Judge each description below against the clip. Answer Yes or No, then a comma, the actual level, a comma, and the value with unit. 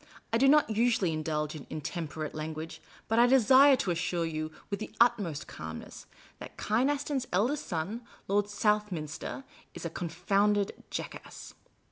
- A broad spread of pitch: Yes, wide, 6.8 semitones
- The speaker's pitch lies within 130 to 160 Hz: No, high, 200 Hz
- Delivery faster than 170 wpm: No, average, 150 wpm